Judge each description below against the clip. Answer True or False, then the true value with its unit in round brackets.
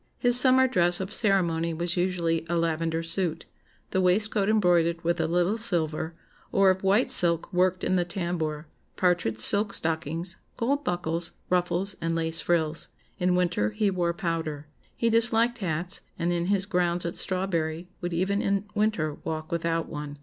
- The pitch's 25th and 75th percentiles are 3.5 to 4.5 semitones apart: False (2.7 semitones)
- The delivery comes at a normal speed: True (165 wpm)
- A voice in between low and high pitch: True (175 Hz)